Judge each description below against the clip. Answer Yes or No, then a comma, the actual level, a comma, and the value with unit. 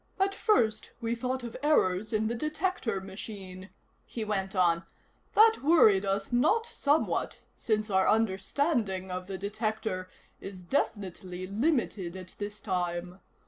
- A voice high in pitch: Yes, high, 210 Hz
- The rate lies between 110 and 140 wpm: Yes, slow, 135 wpm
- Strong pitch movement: No, average, 4.3 semitones